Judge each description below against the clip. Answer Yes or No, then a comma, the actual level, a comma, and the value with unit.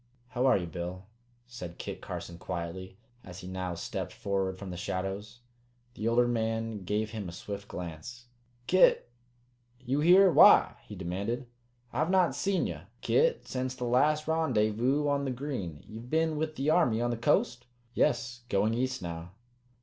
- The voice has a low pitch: Yes, low, 115 Hz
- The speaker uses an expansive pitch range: Yes, wide, 5.8 semitones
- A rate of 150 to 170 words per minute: Yes, average, 165 wpm